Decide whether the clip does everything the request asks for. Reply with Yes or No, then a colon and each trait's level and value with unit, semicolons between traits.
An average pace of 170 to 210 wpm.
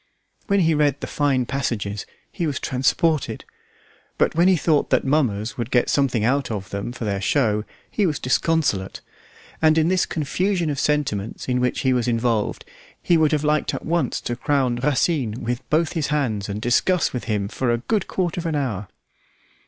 Yes: average, 190 wpm